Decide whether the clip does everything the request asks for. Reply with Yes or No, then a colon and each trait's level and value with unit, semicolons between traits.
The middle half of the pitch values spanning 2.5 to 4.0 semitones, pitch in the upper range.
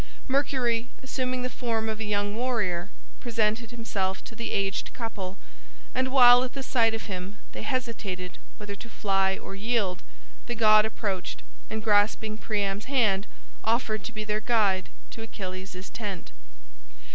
Yes: average, 3.2 semitones; high, 215 Hz